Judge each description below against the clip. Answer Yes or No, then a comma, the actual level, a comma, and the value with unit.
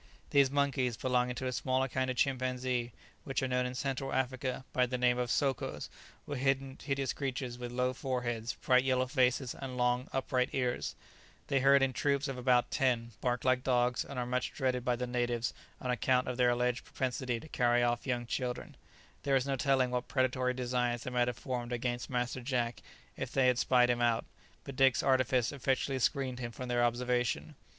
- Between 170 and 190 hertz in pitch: No, low, 125 Hz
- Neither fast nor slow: Yes, average, 195 wpm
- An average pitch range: No, narrow, 1.2 semitones